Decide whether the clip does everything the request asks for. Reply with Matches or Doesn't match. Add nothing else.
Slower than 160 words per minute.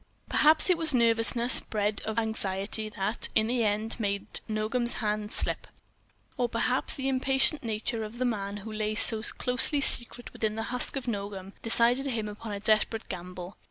Doesn't match